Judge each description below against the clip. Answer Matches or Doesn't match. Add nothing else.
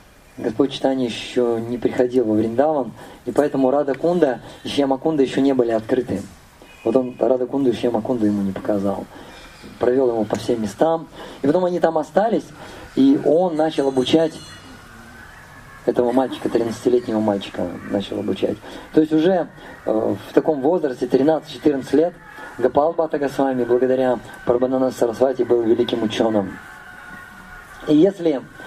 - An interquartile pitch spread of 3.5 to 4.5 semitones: Matches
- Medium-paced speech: Matches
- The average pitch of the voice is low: Matches